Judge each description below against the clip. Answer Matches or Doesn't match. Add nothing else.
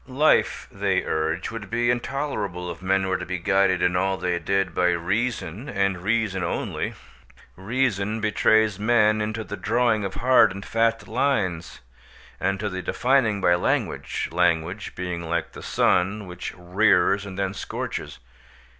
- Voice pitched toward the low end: Matches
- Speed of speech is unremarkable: Matches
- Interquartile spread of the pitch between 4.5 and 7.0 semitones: Doesn't match